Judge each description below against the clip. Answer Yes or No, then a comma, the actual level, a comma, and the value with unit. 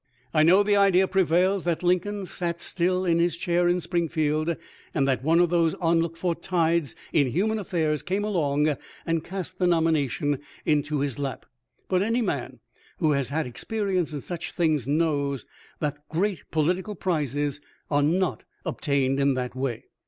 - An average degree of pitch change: Yes, average, 3.8 semitones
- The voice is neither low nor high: Yes, medium, 165 Hz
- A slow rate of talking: No, average, 165 wpm